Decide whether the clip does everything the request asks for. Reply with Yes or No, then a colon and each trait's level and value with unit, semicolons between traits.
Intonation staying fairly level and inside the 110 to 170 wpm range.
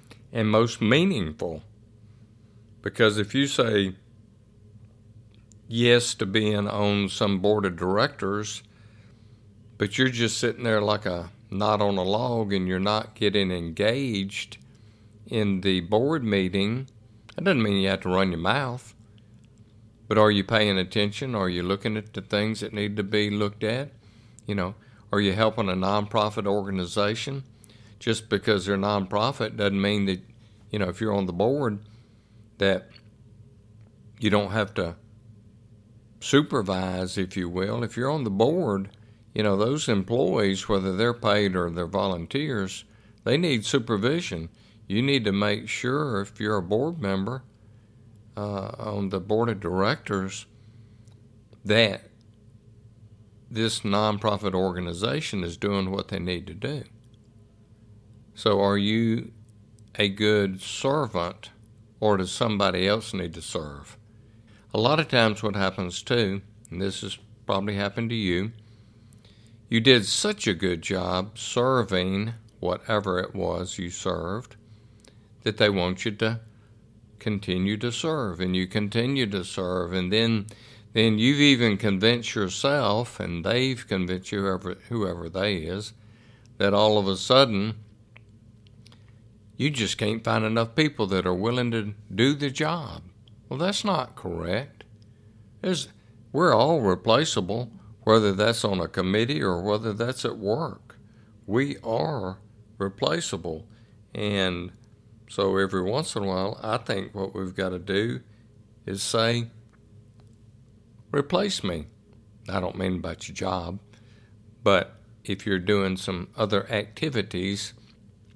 Yes: narrow, 2.3 semitones; average, 140 wpm